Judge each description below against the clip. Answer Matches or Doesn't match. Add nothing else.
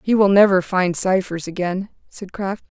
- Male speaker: Doesn't match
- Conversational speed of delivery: Matches